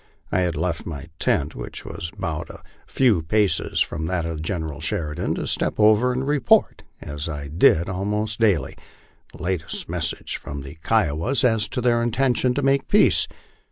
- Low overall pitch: Yes, very low, 90 Hz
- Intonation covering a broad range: Yes, wide, 6.8 semitones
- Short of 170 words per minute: No, average, 175 wpm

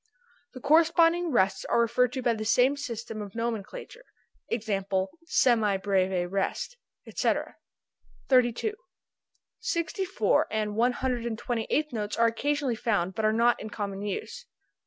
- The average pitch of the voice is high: Yes, high, 235 Hz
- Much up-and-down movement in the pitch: No, average, 4.6 semitones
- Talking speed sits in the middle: Yes, average, 145 wpm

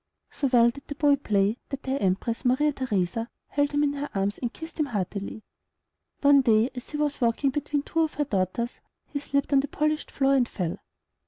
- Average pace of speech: No, fast, 210 wpm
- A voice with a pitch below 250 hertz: No, very high, 270 Hz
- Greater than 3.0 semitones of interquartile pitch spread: Yes, average, 4.2 semitones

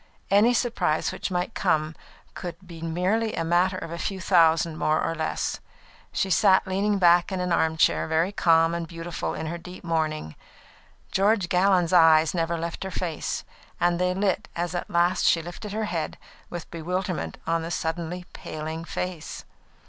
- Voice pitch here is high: No, medium, 175 Hz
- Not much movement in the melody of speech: Yes, narrow, 2.2 semitones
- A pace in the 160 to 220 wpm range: Yes, average, 170 wpm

